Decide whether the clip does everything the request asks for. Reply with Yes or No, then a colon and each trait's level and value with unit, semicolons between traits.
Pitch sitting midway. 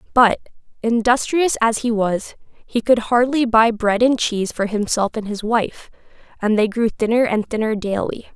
No: high, 225 Hz